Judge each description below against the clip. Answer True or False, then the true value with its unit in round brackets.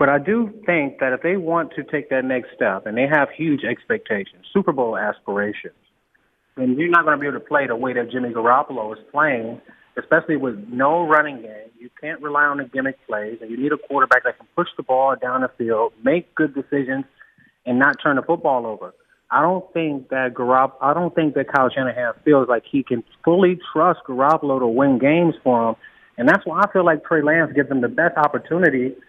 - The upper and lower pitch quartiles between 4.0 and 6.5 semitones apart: True (4.4 semitones)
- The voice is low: False (145 Hz)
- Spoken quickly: True (220 wpm)